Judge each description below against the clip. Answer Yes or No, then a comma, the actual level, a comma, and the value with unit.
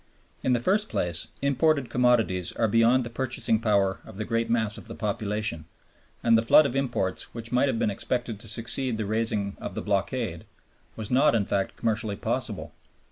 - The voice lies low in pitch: Yes, low, 115 Hz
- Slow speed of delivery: No, average, 190 wpm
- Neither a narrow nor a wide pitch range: Yes, average, 3.0 semitones